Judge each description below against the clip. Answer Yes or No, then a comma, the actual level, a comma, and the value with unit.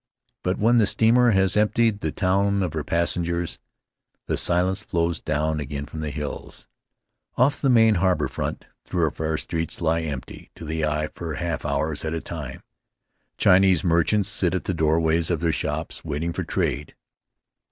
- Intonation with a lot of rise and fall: No, average, 3.6 semitones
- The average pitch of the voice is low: Yes, very low, 85 Hz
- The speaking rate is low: No, average, 165 wpm